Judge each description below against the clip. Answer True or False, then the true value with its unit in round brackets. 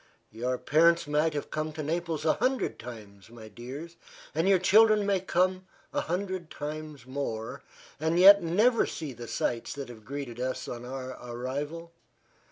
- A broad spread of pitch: True (5.7 semitones)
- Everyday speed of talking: True (165 wpm)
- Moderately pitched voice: True (150 Hz)